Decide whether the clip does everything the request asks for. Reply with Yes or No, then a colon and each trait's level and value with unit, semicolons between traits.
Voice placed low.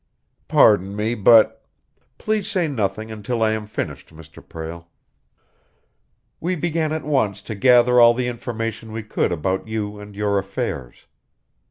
Yes: low, 110 Hz